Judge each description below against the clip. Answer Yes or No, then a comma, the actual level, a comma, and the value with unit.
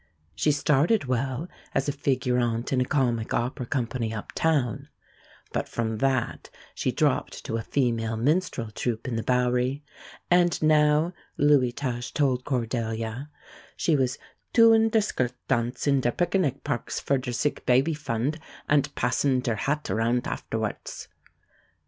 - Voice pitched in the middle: No, low, 130 Hz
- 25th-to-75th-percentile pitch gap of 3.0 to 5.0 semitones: Yes, average, 3.7 semitones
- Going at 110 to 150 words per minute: Yes, average, 145 wpm